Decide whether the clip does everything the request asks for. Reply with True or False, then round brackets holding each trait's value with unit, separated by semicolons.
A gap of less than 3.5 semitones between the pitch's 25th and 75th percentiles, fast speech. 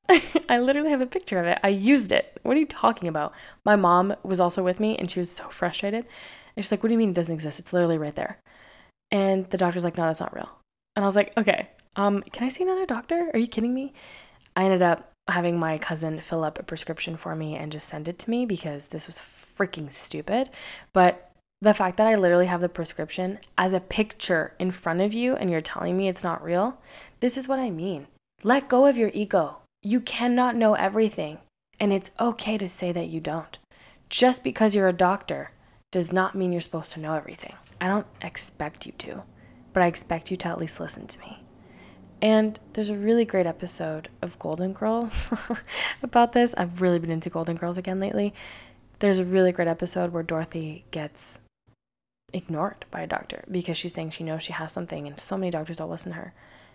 False (4.4 semitones; 220 wpm)